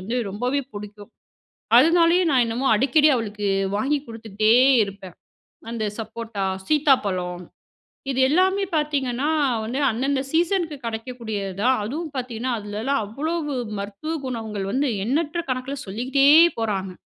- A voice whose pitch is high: Yes, high, 245 Hz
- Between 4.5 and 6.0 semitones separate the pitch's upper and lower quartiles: Yes, wide, 5.5 semitones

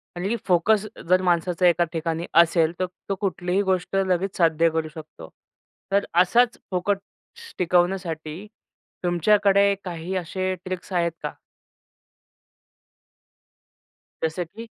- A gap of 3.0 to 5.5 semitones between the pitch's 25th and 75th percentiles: No, narrow, 2.6 semitones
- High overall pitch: No, medium, 180 Hz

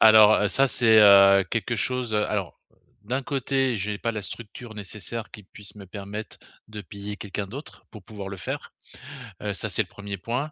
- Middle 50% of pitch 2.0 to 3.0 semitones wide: Yes, narrow, 2.5 semitones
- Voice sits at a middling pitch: No, low, 105 Hz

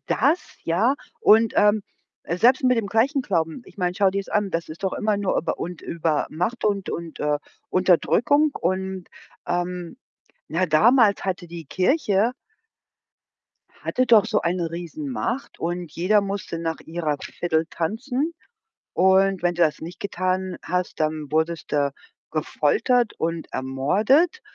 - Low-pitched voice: No, medium, 185 Hz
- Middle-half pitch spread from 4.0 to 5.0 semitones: Yes, average, 4.6 semitones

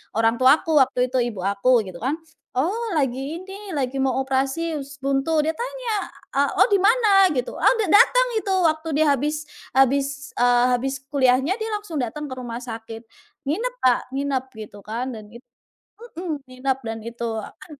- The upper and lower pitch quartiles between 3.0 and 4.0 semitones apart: No, average, 4.7 semitones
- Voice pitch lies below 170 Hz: No, very high, 270 Hz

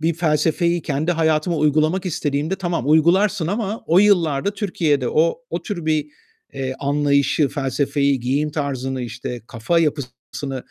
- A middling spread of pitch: Yes, average, 3.6 semitones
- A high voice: No, medium, 150 Hz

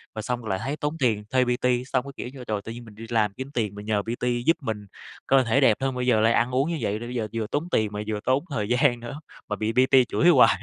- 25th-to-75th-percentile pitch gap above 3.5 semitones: No, average, 3.2 semitones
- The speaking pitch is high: No, low, 120 Hz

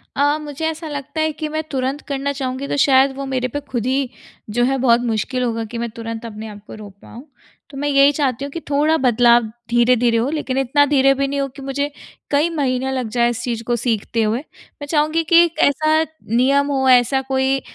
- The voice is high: Yes, very high, 265 Hz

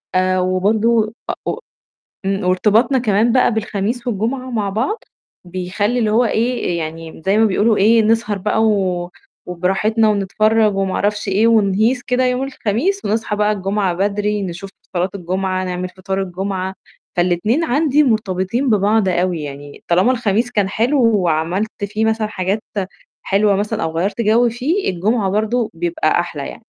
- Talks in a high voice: Yes, high, 205 Hz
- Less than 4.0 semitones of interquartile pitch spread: Yes, average, 3.4 semitones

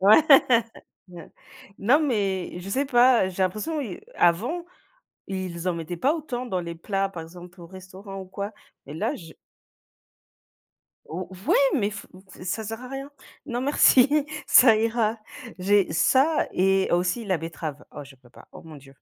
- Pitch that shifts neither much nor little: No, wide, 5.7 semitones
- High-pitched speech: Yes, high, 195 Hz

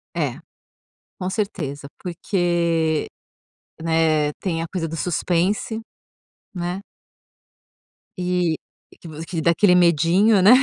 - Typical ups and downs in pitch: No, narrow, 2.0 semitones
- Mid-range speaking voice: Yes, medium, 175 Hz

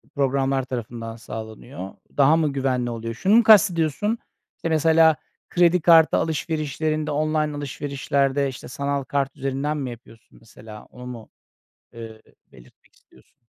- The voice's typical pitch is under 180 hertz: Yes, medium, 140 Hz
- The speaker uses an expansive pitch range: No, average, 4.3 semitones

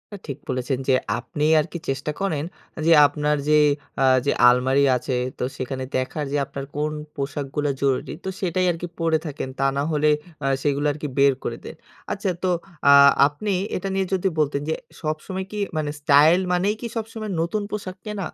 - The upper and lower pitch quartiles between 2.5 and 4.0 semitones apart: No, average, 4.8 semitones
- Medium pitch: Yes, medium, 150 Hz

